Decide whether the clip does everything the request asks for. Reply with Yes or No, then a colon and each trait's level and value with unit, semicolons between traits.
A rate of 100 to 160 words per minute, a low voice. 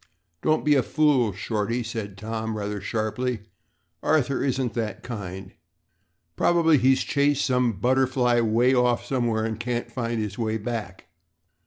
Yes: average, 140 wpm; low, 120 Hz